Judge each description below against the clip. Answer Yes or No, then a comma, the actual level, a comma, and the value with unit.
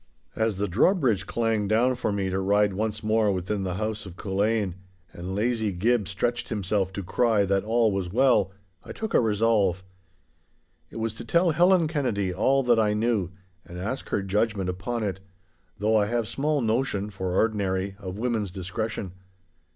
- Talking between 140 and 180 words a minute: Yes, average, 170 wpm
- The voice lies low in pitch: Yes, low, 105 Hz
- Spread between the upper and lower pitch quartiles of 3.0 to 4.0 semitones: Yes, average, 3.3 semitones